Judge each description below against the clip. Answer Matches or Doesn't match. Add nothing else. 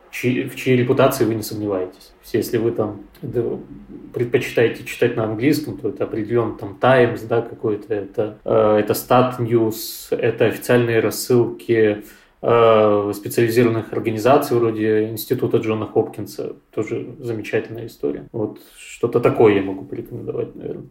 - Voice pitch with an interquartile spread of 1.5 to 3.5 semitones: Matches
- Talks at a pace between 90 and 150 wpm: Matches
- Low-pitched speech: Matches